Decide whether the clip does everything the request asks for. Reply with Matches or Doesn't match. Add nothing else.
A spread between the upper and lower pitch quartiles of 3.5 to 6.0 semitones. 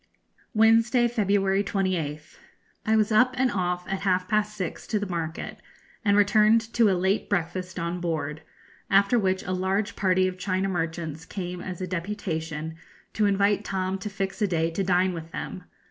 Doesn't match